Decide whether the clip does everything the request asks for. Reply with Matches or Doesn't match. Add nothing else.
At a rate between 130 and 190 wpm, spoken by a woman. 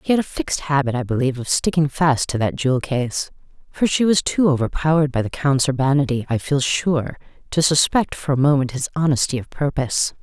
Doesn't match